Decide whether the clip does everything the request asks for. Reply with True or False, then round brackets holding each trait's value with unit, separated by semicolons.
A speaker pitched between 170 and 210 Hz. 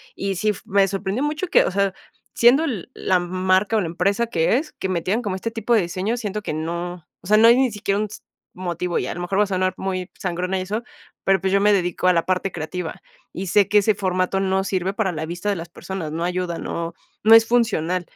True (190 Hz)